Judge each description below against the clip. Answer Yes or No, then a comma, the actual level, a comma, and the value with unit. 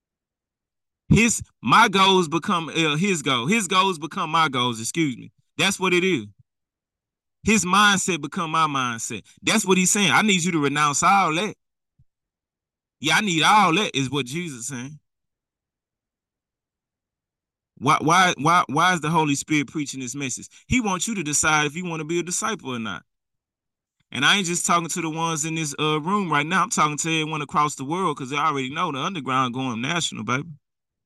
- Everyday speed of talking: Yes, average, 190 wpm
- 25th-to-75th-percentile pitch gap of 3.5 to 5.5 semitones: Yes, average, 5.0 semitones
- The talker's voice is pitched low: No, medium, 160 Hz